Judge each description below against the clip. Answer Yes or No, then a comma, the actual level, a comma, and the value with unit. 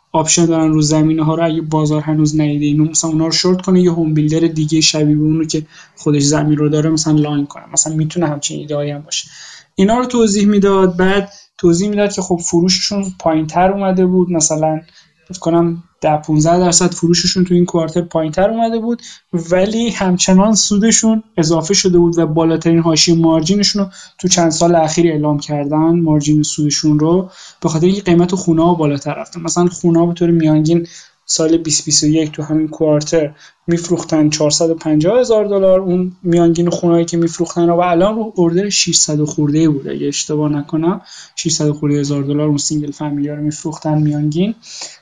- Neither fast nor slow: No, fast, 175 wpm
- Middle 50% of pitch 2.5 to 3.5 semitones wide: Yes, average, 2.8 semitones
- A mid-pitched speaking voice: Yes, medium, 165 Hz